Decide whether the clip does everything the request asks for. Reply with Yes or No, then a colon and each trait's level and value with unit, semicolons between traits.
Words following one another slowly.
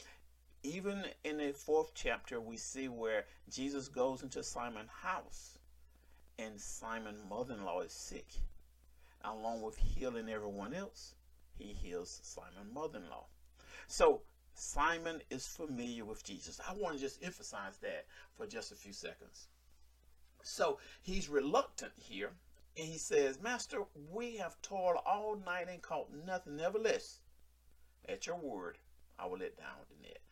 No: average, 145 wpm